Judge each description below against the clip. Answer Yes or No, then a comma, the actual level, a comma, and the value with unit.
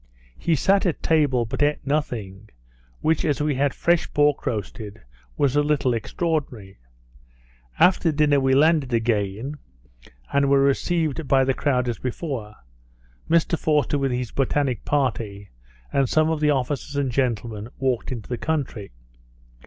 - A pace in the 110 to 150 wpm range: Yes, average, 145 wpm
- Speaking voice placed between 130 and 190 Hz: Yes, low, 135 Hz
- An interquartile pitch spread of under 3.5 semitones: No, average, 3.9 semitones